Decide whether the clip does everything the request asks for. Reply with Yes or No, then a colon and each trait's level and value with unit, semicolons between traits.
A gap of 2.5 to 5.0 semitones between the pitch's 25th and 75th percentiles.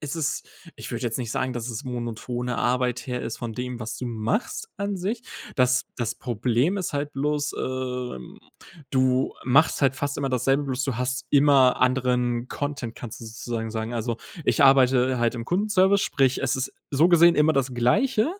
Yes: average, 2.9 semitones